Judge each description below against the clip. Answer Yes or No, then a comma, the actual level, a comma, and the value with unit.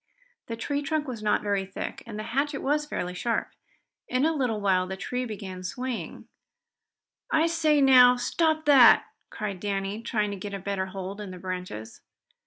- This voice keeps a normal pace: Yes, average, 180 wpm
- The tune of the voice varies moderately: No, wide, 5.8 semitones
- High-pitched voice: Yes, high, 215 Hz